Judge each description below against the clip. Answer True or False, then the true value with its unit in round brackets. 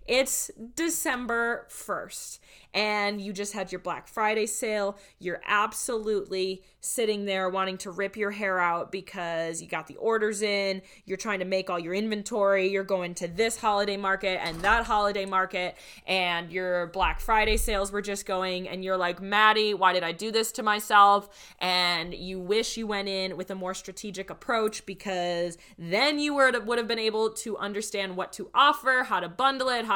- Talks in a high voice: True (200 Hz)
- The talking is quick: False (180 wpm)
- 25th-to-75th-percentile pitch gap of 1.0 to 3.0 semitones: True (2.7 semitones)